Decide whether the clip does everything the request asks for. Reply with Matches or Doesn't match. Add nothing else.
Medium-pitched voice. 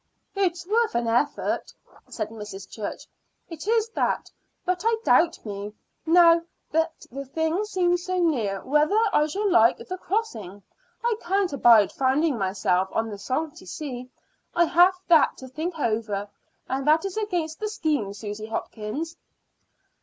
Doesn't match